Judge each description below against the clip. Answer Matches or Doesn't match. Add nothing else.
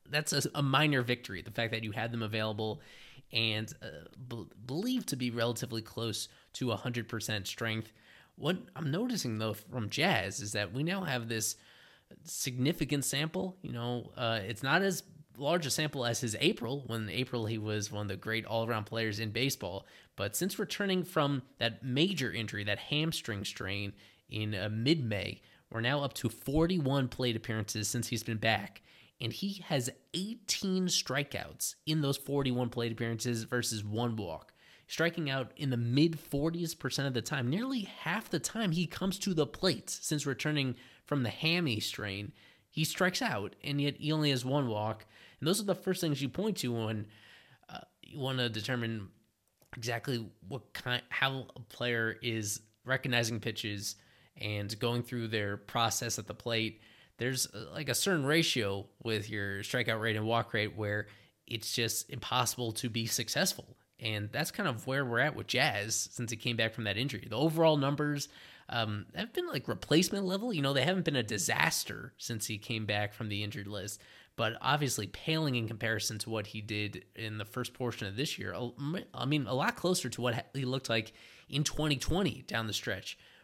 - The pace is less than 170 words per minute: Doesn't match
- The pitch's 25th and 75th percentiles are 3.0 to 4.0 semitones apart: Doesn't match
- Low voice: Matches